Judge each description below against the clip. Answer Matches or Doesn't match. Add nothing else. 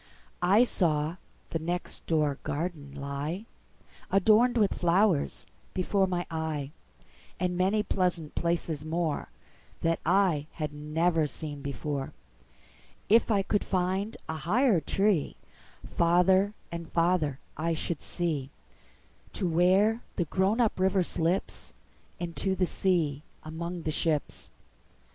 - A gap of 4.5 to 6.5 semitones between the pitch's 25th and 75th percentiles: Doesn't match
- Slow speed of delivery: Matches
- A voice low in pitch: Doesn't match